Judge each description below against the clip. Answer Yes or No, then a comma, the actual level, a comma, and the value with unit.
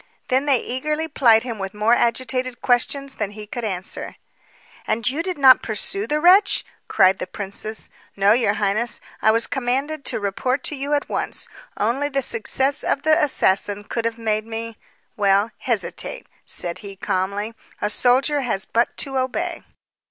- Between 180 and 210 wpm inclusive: No, average, 165 wpm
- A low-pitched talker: No, high, 240 Hz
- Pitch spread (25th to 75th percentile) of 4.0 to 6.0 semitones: Yes, average, 4.7 semitones